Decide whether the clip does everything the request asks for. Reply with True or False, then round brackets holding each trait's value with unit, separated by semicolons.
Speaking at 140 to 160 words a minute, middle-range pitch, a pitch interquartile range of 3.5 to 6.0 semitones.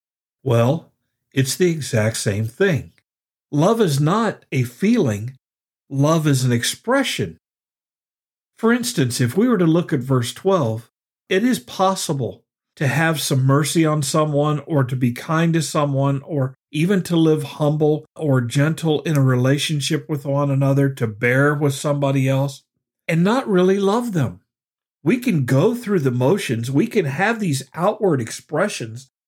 True (155 wpm; 145 Hz; 4.1 semitones)